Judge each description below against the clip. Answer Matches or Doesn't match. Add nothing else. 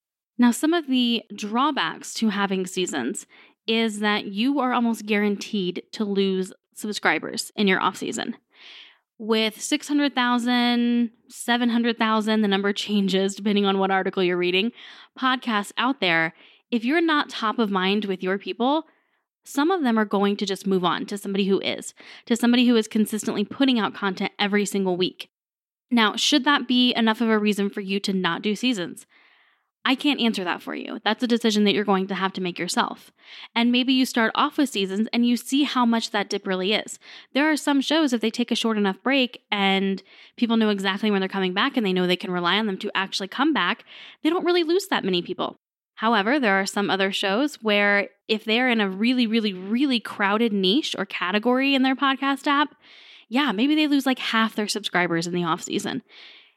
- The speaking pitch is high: Matches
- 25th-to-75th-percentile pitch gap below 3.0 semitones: Doesn't match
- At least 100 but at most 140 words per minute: Doesn't match